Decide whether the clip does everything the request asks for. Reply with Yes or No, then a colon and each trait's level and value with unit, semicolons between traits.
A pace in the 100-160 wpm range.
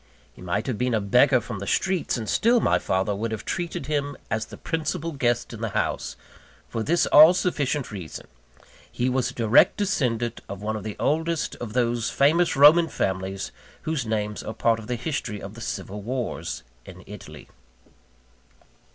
No: average, 180 wpm